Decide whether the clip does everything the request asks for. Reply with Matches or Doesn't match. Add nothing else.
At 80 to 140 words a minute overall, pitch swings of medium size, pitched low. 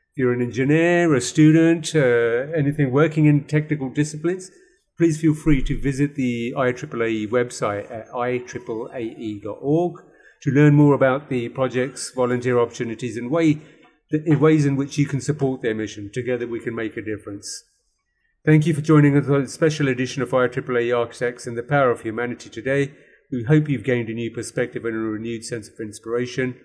Doesn't match